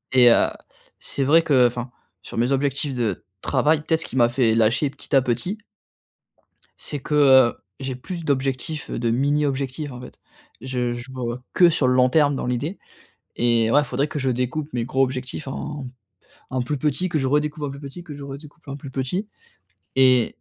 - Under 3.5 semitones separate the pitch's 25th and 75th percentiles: Yes, average, 2.9 semitones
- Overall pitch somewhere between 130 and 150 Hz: Yes, low, 135 Hz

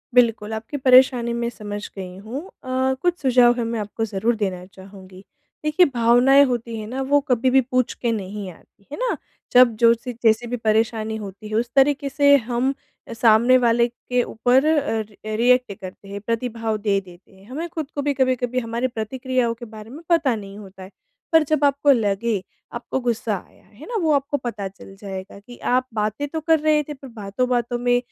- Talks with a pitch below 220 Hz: No, high, 235 Hz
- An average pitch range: Yes, average, 3.5 semitones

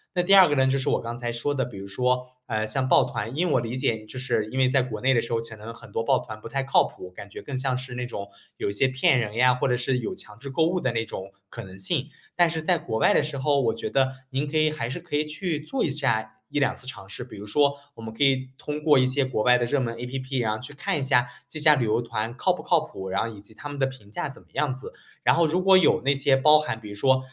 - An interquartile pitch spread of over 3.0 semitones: Yes, average, 3.9 semitones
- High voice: No, low, 130 Hz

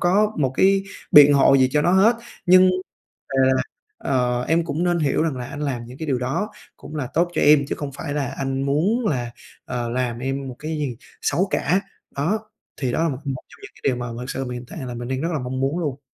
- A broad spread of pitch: No, average, 4.6 semitones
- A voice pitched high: No, medium, 140 Hz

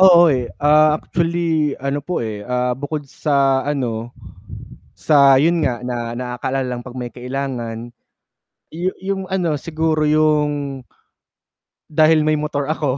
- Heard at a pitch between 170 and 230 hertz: No, medium, 145 Hz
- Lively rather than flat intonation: No, average, 3.5 semitones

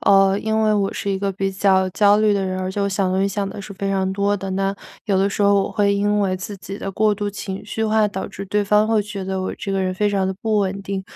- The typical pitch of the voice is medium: No, high, 200 Hz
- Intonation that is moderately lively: No, narrow, 1.3 semitones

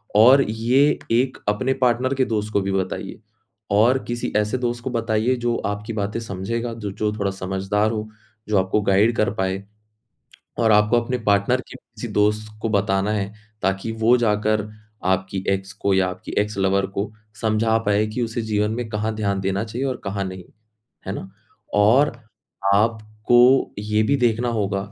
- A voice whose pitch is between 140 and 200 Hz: No, low, 105 Hz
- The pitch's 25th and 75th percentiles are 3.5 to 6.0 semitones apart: No, average, 2.8 semitones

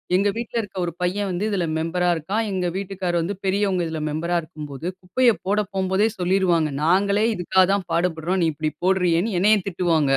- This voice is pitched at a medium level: Yes, medium, 180 Hz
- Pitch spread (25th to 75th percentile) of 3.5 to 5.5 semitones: No, average, 2.7 semitones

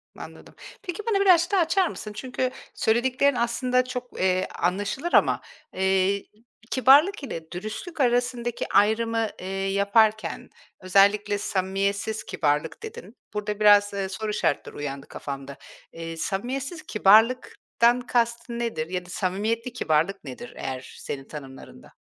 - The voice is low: No, high, 215 Hz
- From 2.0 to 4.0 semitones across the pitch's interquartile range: No, average, 4.8 semitones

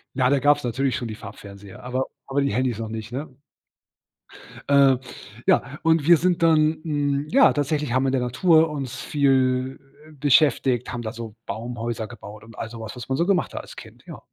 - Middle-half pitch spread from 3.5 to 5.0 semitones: Yes, average, 3.8 semitones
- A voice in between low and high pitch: No, low, 130 Hz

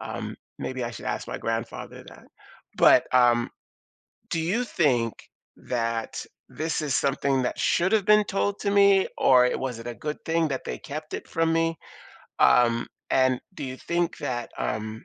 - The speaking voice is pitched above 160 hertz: No, low, 135 Hz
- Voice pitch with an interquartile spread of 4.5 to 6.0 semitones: Yes, wide, 5.5 semitones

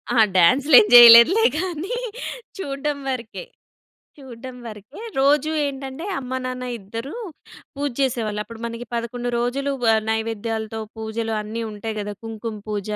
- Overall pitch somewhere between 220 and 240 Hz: Yes, high, 235 Hz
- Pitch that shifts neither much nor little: Yes, average, 3.7 semitones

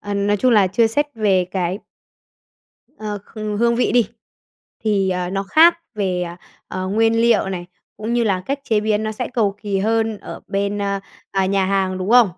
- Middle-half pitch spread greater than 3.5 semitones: No, average, 2.7 semitones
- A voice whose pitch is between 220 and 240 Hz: No, high, 205 Hz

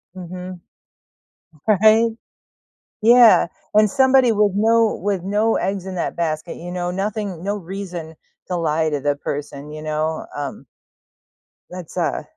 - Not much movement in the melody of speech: No, average, 4.6 semitones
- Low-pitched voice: No, medium, 185 Hz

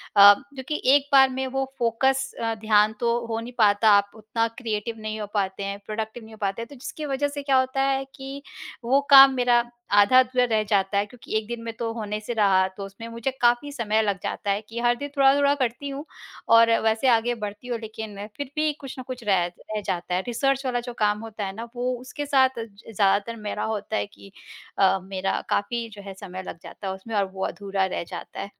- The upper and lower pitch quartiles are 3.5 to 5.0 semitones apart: Yes, average, 4.0 semitones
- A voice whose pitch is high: Yes, high, 225 Hz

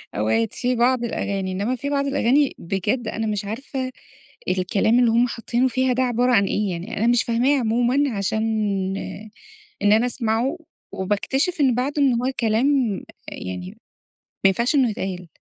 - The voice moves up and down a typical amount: Yes, average, 4.1 semitones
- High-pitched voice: Yes, high, 235 Hz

